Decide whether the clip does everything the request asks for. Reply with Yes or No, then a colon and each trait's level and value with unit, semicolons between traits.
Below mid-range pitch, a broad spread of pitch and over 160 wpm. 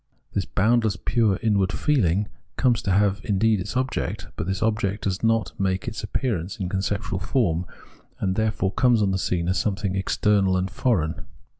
No: low, 100 Hz; average, 2.9 semitones; average, 175 wpm